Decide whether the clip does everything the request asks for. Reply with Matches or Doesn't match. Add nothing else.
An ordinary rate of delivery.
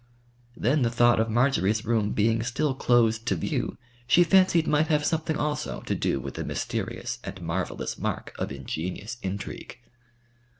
Matches